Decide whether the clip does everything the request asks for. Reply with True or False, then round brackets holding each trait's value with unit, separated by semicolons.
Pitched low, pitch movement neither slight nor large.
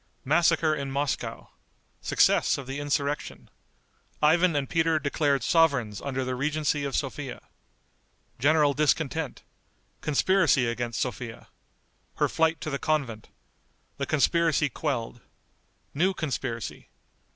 False (145 Hz; 3.0 semitones)